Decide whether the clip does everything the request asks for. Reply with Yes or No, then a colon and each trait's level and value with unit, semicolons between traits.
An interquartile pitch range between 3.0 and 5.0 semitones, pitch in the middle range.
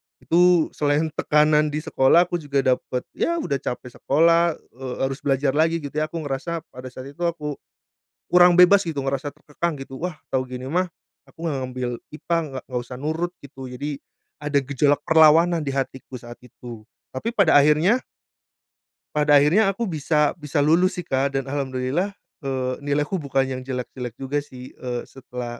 Yes: average, 3.6 semitones; medium, 145 Hz